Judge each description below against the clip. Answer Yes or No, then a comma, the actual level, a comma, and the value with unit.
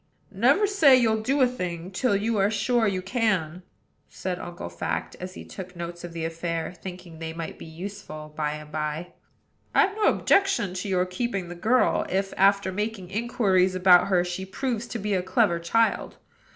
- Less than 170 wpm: No, average, 185 wpm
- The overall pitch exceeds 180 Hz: Yes, high, 190 Hz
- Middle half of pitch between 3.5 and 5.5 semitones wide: Yes, average, 4.2 semitones